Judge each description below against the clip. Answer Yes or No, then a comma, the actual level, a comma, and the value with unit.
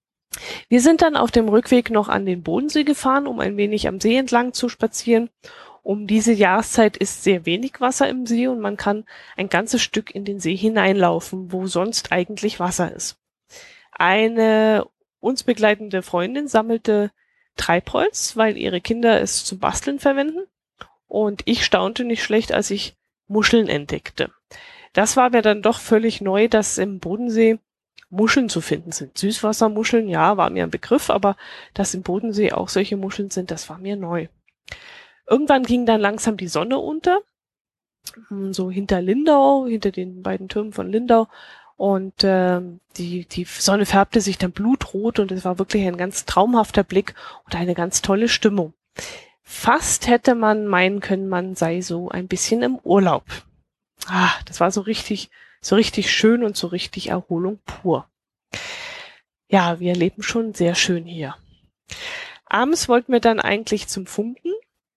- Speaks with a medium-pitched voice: No, high, 215 Hz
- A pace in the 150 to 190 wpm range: Yes, average, 160 wpm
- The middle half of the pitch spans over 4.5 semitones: No, average, 4.1 semitones